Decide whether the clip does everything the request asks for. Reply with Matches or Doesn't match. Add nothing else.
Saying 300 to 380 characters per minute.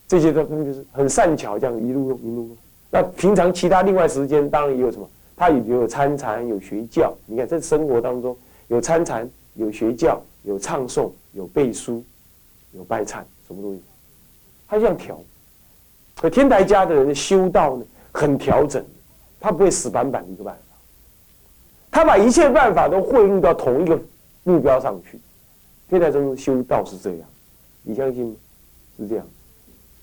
Doesn't match